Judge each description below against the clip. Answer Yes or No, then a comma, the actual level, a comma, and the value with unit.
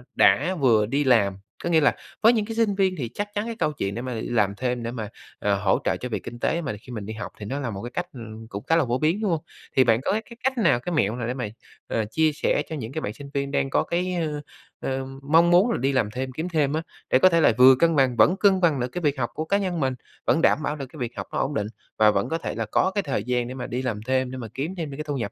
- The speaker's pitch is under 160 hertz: Yes, low, 135 Hz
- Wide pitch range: Yes, wide, 5.7 semitones